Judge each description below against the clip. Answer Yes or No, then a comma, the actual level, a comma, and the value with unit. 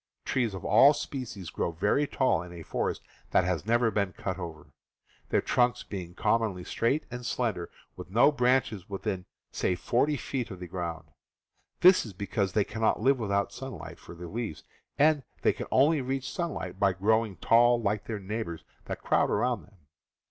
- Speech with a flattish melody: No, average, 5.1 semitones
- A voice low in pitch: Yes, low, 105 Hz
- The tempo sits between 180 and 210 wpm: Yes, average, 185 wpm